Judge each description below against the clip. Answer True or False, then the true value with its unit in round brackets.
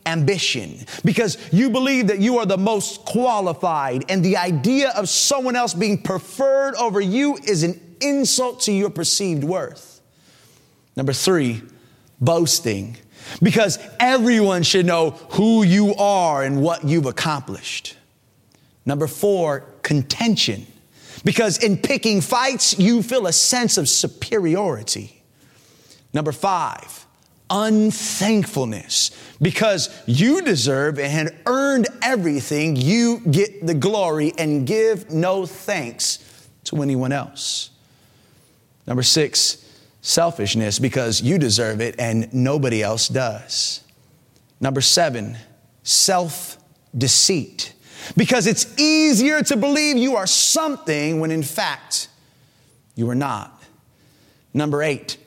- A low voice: False (165 Hz)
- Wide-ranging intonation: True (7.7 semitones)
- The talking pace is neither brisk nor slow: False (115 wpm)